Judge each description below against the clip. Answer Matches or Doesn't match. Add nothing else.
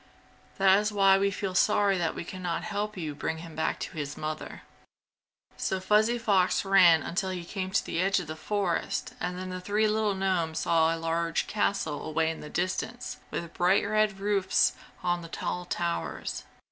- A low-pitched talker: Doesn't match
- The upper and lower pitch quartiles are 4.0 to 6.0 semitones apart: Doesn't match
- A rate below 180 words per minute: Doesn't match